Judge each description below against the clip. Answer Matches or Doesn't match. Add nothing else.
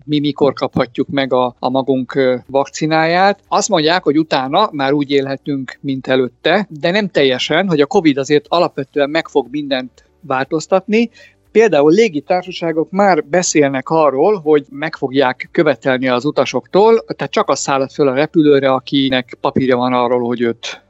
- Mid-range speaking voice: Matches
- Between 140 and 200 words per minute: Matches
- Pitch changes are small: Doesn't match